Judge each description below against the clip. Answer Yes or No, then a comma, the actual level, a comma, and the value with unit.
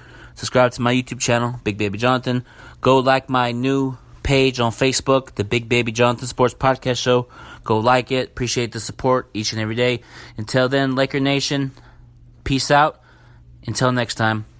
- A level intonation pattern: Yes, narrow, 1.8 semitones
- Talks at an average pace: Yes, average, 170 wpm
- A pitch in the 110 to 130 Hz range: Yes, low, 125 Hz